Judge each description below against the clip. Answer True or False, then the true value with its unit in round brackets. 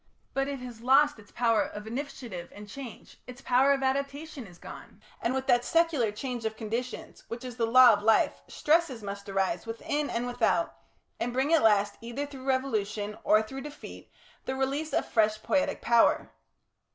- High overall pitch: True (245 Hz)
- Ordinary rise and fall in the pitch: True (3.9 semitones)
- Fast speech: False (180 wpm)